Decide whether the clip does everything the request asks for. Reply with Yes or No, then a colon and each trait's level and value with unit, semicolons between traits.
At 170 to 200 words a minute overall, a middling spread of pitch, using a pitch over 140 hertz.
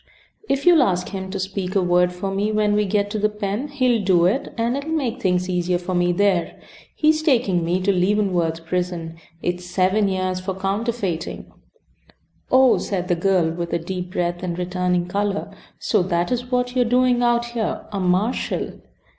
Yes: average, 190 wpm; average, 4.1 semitones; high, 190 Hz